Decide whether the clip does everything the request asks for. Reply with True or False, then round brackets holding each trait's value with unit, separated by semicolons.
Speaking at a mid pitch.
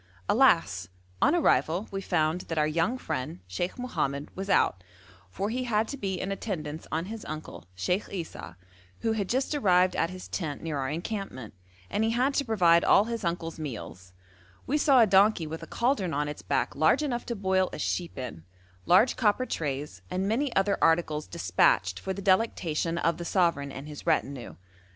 True (180 Hz)